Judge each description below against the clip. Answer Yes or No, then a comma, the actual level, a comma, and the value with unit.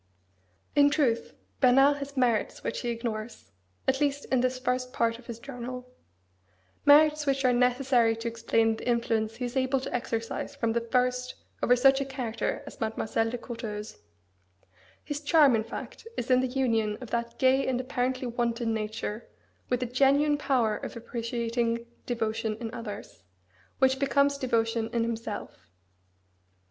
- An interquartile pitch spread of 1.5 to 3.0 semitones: Yes, narrow, 2.6 semitones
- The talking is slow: No, average, 155 wpm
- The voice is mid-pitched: No, high, 245 Hz